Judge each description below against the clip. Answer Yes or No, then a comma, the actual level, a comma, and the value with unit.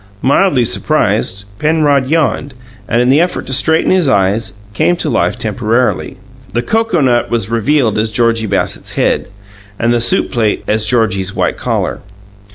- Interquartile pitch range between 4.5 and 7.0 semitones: Yes, average, 4.9 semitones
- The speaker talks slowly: No, average, 155 wpm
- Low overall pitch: Yes, low, 120 Hz